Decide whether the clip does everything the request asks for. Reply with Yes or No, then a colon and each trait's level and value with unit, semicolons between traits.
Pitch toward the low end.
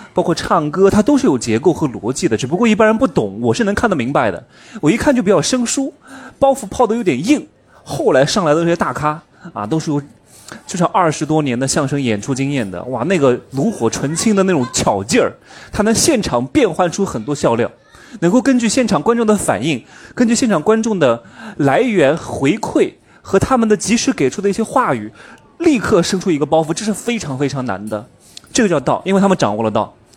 No: high, 190 Hz